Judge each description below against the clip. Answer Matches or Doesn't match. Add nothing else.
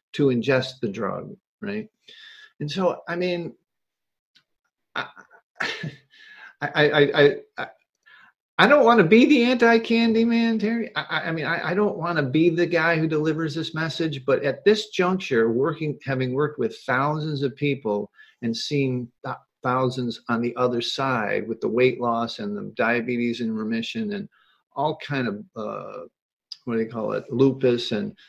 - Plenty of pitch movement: Matches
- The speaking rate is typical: Matches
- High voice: Doesn't match